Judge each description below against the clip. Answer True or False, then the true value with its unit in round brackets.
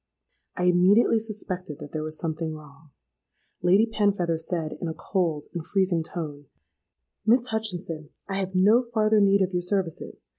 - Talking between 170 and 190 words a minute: False (155 wpm)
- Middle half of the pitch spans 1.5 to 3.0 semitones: False (4.1 semitones)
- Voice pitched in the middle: True (180 Hz)